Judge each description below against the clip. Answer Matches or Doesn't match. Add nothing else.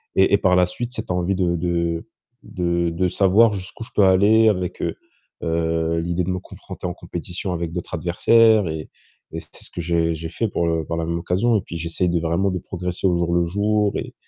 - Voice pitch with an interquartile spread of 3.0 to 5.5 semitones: Doesn't match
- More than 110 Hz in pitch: Doesn't match